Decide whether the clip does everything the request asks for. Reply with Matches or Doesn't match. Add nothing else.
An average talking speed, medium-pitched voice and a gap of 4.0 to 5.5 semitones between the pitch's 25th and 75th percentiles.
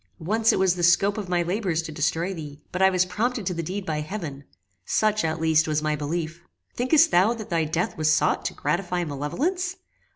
Doesn't match